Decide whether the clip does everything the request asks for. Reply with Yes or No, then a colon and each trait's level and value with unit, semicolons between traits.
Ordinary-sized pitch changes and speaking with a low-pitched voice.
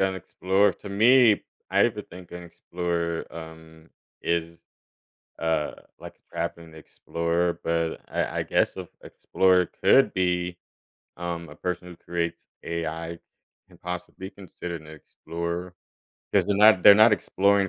No: narrow, 2.3 semitones; very low, 90 Hz